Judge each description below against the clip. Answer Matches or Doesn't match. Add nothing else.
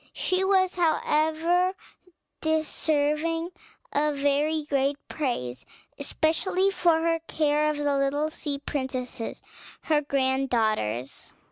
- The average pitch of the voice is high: Matches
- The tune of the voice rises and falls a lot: Doesn't match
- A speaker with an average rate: Doesn't match